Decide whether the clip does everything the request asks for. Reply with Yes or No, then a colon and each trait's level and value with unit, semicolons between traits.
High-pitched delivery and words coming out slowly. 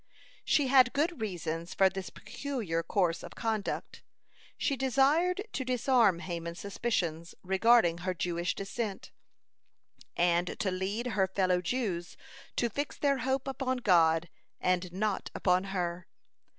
Yes: high, 195 Hz; slow, 130 wpm